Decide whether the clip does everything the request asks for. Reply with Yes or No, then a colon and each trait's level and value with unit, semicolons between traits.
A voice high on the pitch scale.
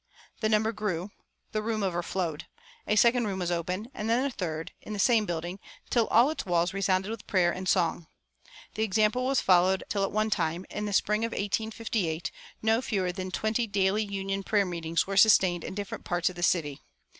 Yes: high, 195 Hz